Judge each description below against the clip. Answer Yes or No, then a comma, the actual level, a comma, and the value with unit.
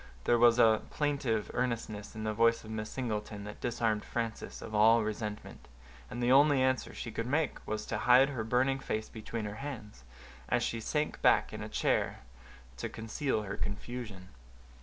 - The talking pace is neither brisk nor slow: Yes, average, 180 wpm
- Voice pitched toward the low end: Yes, low, 115 Hz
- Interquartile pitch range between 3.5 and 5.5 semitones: No, average, 2.7 semitones